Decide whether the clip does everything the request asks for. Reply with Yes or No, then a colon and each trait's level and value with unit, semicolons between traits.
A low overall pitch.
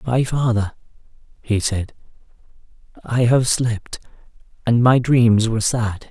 Yes: low, 115 Hz